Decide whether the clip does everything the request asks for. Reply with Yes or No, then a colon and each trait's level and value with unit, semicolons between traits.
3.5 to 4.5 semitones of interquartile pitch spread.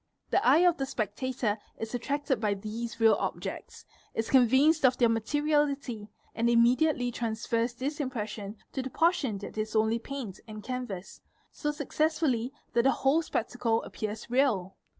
Yes: average, 3.9 semitones